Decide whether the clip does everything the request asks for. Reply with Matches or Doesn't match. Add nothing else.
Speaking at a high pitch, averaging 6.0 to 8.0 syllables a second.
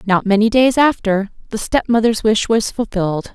Doesn't match